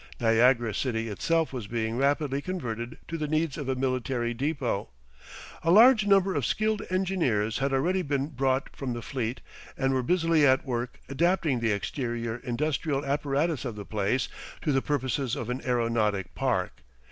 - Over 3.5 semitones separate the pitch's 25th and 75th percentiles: Yes, average, 4.6 semitones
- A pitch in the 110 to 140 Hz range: Yes, low, 135 Hz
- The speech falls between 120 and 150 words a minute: No, average, 165 wpm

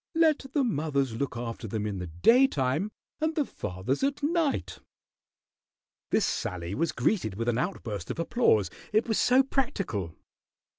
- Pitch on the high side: No, medium, 145 Hz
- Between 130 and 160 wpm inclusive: Yes, average, 150 wpm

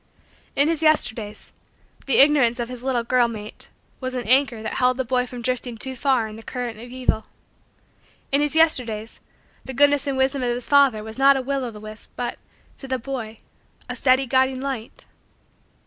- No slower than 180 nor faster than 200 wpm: Yes, average, 195 wpm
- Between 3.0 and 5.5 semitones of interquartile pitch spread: No, narrow, 2.6 semitones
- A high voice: Yes, very high, 255 Hz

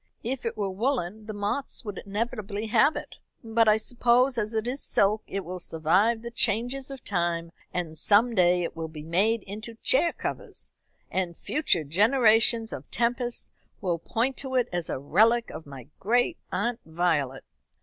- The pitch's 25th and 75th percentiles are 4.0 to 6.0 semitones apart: Yes, average, 5.1 semitones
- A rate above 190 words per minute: No, average, 170 wpm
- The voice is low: No, high, 215 Hz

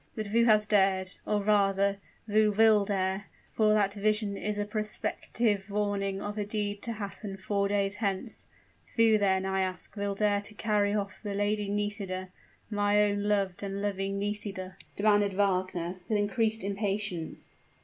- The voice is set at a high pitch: Yes, high, 205 Hz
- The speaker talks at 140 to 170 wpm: Yes, average, 160 wpm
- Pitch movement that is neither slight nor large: No, narrow, 1.2 semitones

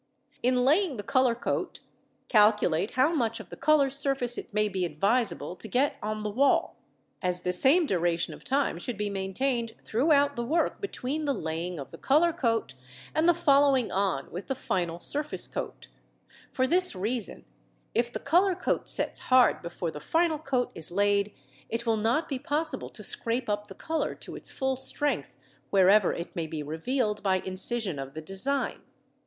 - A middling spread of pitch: No, wide, 6.4 semitones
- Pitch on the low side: No, high, 235 Hz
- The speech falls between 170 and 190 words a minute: Yes, average, 180 wpm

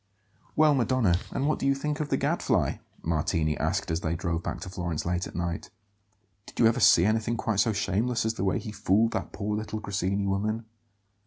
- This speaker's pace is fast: Yes, fast, 210 wpm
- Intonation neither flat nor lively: Yes, average, 4.4 semitones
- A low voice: Yes, low, 105 Hz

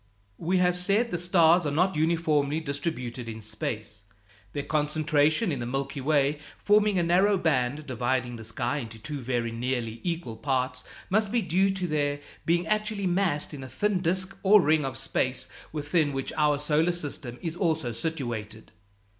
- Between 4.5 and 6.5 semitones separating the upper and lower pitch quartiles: Yes, wide, 5.4 semitones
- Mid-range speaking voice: Yes, medium, 150 Hz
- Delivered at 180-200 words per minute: No, average, 170 wpm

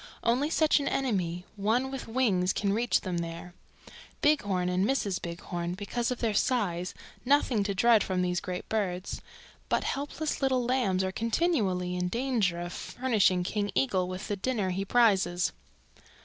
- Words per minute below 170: Yes, average, 160 wpm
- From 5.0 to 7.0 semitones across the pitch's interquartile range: Yes, wide, 5.4 semitones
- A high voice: Yes, high, 205 Hz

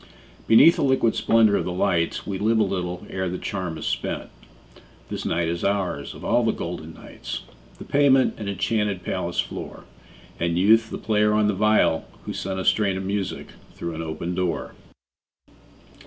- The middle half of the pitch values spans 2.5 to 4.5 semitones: Yes, average, 3.5 semitones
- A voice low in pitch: Yes, low, 100 Hz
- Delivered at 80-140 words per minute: No, average, 180 wpm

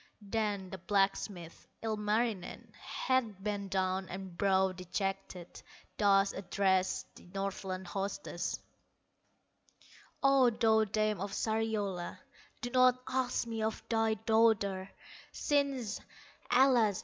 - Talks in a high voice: Yes, high, 205 Hz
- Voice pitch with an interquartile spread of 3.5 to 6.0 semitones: No, average, 2.7 semitones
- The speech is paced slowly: Yes, slow, 100 wpm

